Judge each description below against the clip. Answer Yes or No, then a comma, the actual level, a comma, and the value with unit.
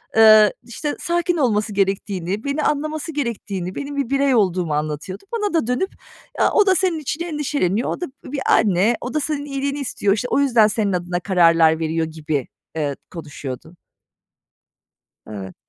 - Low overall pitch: No, high, 220 Hz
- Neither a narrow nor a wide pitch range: No, wide, 8.4 semitones